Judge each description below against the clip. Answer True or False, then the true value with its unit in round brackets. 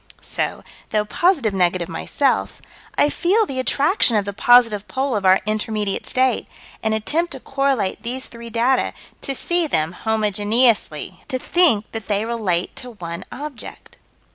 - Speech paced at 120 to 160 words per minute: True (150 wpm)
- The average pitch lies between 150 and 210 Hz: False (230 Hz)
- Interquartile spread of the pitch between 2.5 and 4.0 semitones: False (4.5 semitones)